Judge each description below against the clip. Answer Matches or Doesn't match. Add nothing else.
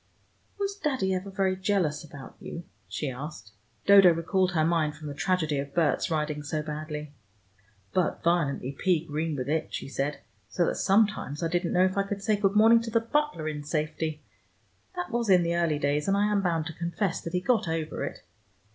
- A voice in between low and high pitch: Matches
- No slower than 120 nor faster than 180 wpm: Doesn't match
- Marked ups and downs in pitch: Doesn't match